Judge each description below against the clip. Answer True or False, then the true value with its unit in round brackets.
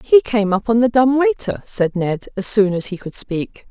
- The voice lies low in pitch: False (220 Hz)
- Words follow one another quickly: True (245 wpm)